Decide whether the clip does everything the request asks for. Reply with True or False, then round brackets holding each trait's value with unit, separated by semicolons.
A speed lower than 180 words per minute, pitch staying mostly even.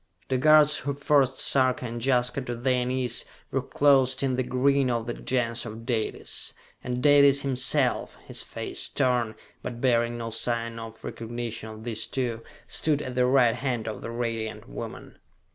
True (170 wpm; 2.3 semitones)